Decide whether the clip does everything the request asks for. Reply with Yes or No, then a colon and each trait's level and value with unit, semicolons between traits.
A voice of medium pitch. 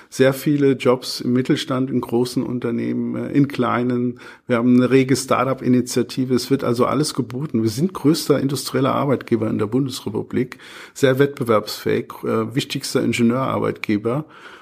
No: low, 125 Hz